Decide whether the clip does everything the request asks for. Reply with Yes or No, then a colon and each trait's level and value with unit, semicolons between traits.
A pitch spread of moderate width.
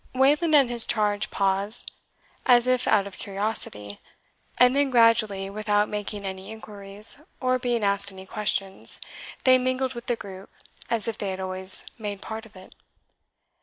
Yes: average, 3.6 semitones